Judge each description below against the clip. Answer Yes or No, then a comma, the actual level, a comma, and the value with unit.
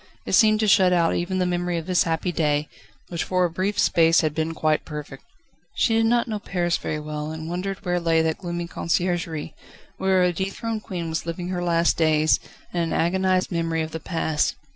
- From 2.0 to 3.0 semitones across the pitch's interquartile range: Yes, narrow, 2.4 semitones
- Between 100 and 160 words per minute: No, fast, 205 wpm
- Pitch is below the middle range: No, medium, 175 Hz